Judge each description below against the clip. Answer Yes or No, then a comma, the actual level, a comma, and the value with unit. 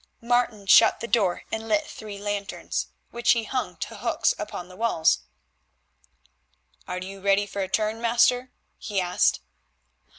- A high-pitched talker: Yes, high, 210 Hz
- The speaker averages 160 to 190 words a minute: No, average, 145 wpm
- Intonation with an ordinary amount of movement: Yes, average, 3.1 semitones